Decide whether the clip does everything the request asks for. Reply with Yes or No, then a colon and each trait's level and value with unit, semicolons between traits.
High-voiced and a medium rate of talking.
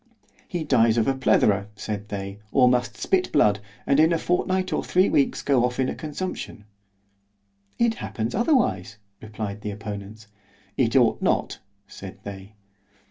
No: low, 115 Hz; average, 145 wpm